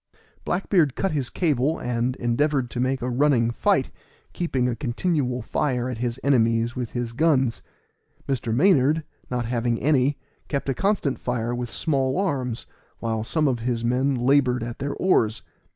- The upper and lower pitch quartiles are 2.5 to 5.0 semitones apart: Yes, average, 3.1 semitones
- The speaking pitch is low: Yes, low, 125 Hz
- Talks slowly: No, average, 165 wpm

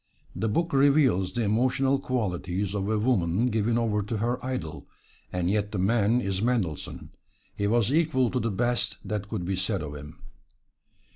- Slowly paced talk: No, average, 170 wpm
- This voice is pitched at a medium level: No, low, 110 Hz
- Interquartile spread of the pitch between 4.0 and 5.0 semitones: Yes, average, 4.3 semitones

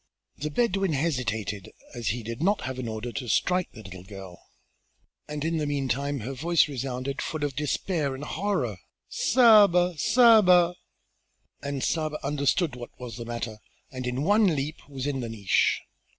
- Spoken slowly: No, average, 165 wpm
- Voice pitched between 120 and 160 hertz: Yes, medium, 140 Hz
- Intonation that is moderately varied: No, wide, 5.7 semitones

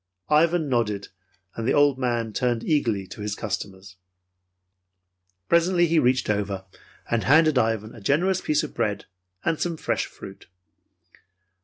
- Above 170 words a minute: No, average, 140 wpm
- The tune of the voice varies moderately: No, wide, 6.7 semitones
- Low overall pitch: Yes, low, 120 Hz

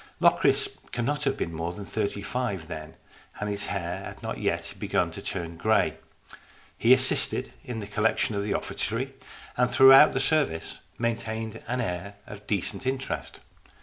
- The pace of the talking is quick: No, average, 160 wpm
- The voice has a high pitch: No, low, 110 Hz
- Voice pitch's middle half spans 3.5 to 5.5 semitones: Yes, average, 4.5 semitones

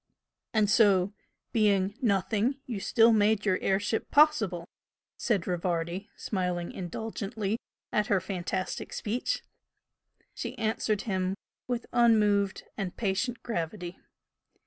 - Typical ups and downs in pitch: Yes, average, 3.0 semitones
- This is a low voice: No, high, 205 Hz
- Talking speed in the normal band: No, slow, 110 wpm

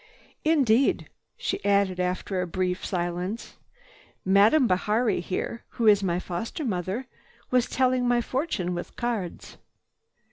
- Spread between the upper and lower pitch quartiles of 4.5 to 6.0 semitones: Yes, average, 5.0 semitones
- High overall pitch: Yes, high, 200 Hz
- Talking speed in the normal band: No, slow, 120 wpm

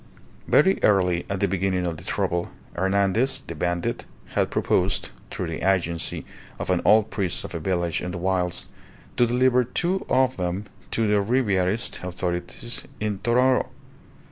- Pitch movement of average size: Yes, average, 4.3 semitones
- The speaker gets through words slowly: No, average, 155 wpm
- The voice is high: No, very low, 95 Hz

